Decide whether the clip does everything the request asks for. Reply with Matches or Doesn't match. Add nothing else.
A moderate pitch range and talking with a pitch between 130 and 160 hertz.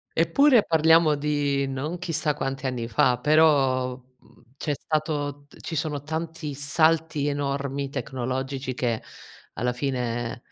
Matches